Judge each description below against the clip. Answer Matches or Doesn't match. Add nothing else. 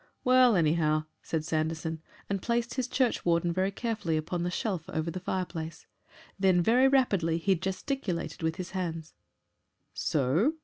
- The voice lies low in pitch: Doesn't match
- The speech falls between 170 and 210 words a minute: Doesn't match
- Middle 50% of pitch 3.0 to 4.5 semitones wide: Doesn't match